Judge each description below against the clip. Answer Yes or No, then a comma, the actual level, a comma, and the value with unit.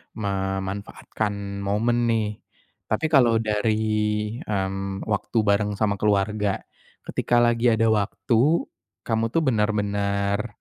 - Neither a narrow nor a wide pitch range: No, narrow, 2.0 semitones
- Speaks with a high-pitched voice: No, low, 105 Hz